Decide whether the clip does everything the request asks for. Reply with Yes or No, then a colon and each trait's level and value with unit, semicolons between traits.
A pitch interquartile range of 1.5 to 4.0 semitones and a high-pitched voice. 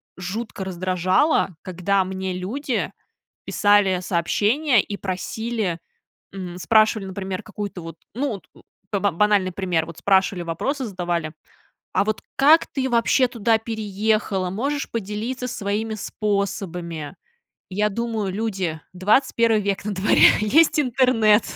Yes: average, 3.5 semitones; high, 205 Hz